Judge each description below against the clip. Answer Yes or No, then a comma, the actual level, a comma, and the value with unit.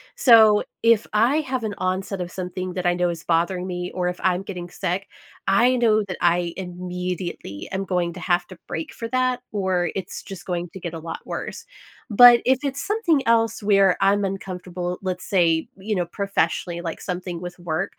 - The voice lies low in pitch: No, medium, 185 Hz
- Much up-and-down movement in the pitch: No, average, 2.9 semitones